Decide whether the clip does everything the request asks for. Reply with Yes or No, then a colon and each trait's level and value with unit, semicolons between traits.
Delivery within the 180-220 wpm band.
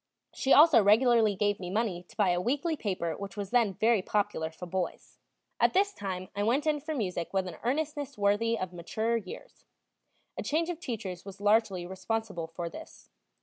Yes: average, 190 wpm